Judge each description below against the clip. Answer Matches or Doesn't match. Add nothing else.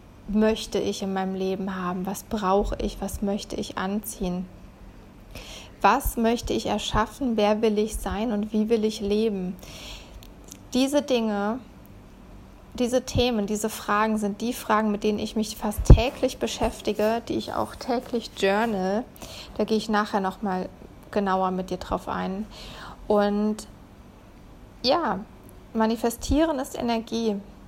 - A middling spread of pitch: Doesn't match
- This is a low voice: Doesn't match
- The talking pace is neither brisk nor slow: Matches